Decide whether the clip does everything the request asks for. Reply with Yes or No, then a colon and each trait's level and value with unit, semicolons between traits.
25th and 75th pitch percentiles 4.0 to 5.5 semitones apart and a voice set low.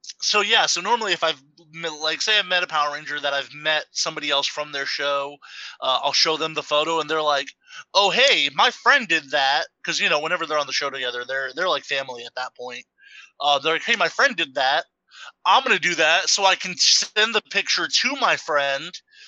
No: average, 5.0 semitones; medium, 160 Hz